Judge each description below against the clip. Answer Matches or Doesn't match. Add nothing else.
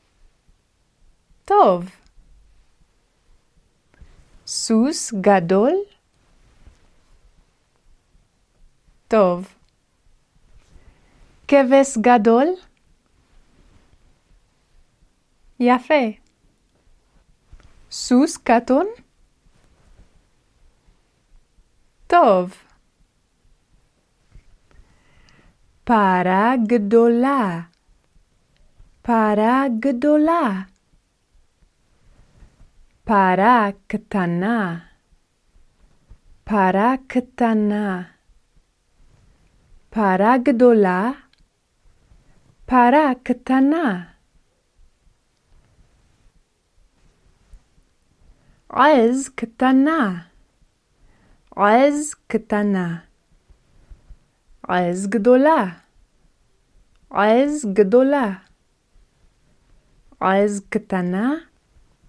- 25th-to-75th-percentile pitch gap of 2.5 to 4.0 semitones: Doesn't match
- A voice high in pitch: Matches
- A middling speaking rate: Doesn't match